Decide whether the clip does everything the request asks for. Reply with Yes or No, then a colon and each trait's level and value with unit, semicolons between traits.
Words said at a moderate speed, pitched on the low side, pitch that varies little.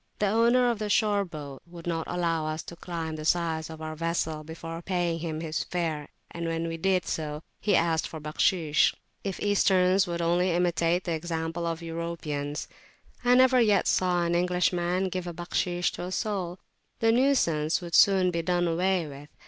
No: average, 180 wpm; medium, 170 Hz; narrow, 2.2 semitones